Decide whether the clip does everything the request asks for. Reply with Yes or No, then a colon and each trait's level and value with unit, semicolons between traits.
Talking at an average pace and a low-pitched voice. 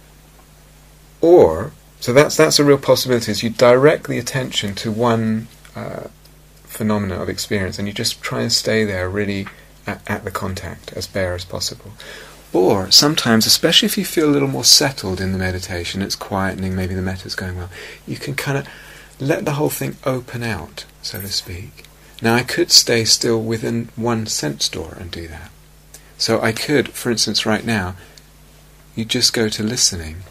Yes: average, 180 wpm; low, 110 Hz